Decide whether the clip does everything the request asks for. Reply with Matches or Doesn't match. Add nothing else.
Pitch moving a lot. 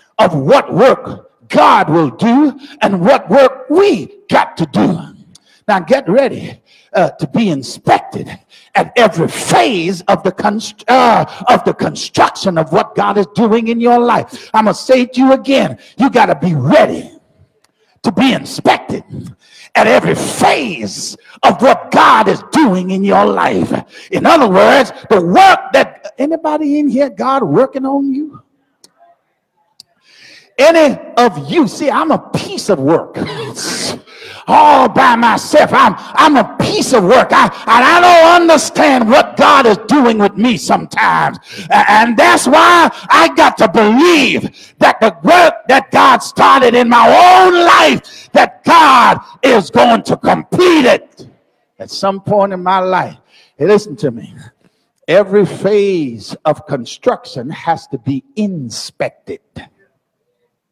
Matches